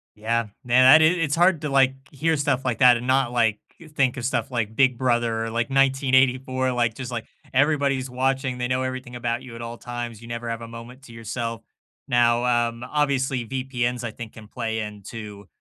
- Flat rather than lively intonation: Yes, narrow, 2.2 semitones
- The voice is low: Yes, low, 125 Hz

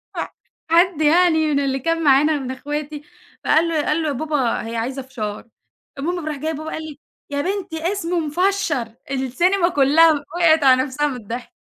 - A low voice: No, very high, 300 Hz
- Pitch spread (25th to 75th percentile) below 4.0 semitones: Yes, average, 3.5 semitones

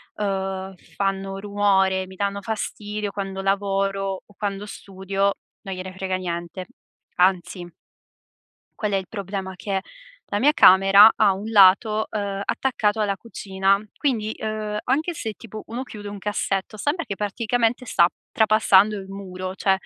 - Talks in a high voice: Yes, high, 200 Hz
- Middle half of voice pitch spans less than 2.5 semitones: Yes, narrow, 1.8 semitones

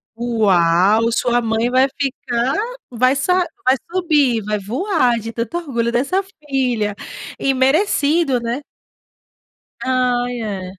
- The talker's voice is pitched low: No, high, 245 Hz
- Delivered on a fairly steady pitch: No, average, 3.2 semitones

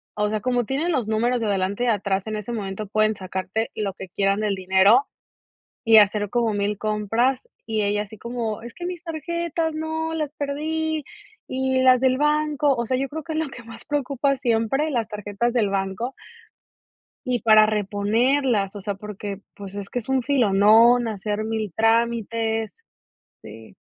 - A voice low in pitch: No, high, 225 Hz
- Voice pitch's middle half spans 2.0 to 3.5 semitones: No, average, 4.4 semitones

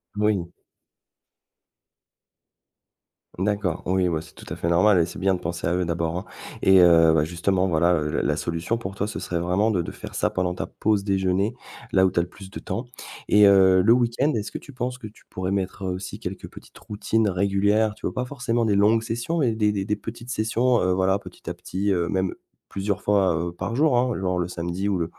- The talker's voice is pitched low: Yes, very low, 95 Hz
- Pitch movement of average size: Yes, average, 3.2 semitones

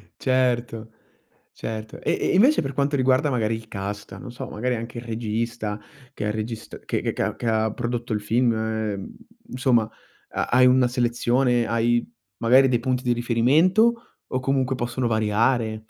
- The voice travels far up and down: No, narrow, 2.6 semitones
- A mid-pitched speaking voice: No, low, 120 Hz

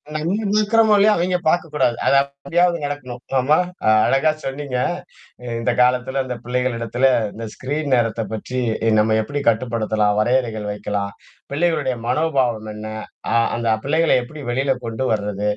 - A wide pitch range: No, average, 4.8 semitones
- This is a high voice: No, low, 130 Hz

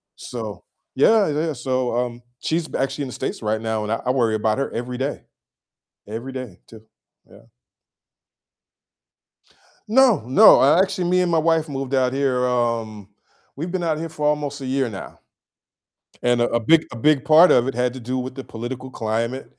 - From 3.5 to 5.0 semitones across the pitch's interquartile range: Yes, average, 4.4 semitones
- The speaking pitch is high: No, low, 130 Hz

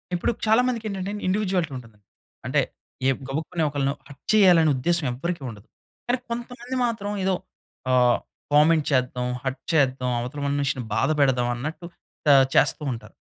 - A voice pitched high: No, medium, 150 Hz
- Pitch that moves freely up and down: Yes, wide, 6.5 semitones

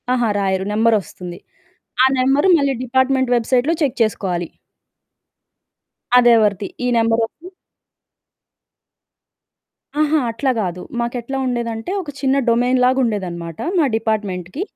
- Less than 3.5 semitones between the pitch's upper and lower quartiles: No, average, 4.1 semitones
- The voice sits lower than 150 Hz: No, high, 230 Hz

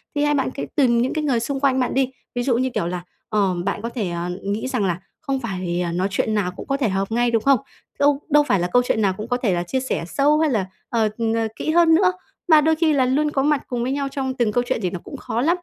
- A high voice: Yes, high, 245 Hz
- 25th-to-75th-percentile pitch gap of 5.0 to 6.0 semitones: Yes, average, 5.3 semitones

